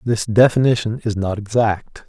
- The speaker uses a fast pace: No, average, 145 wpm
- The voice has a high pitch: No, low, 110 Hz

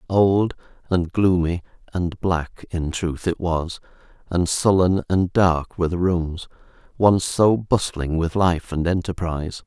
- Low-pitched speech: Yes, very low, 90 Hz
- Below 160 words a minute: Yes, average, 145 wpm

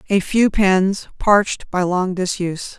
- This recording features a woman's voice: Yes, female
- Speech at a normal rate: Yes, average, 150 wpm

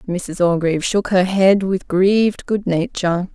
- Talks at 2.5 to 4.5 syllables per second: Yes, 4.4 syllables/s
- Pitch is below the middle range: No, medium, 185 Hz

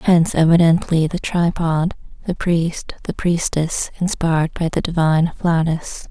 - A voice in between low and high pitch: Yes, medium, 165 Hz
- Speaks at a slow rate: Yes, slow, 130 wpm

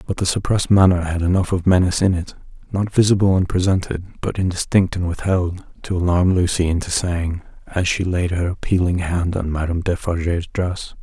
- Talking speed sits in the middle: Yes, average, 170 wpm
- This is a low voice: Yes, very low, 90 Hz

